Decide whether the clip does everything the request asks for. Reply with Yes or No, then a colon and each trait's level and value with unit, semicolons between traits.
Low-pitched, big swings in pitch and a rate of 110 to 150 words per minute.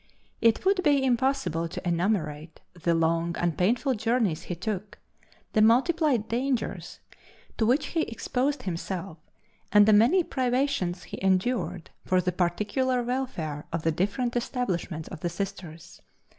No: high, 205 Hz; wide, 6.5 semitones; average, 140 wpm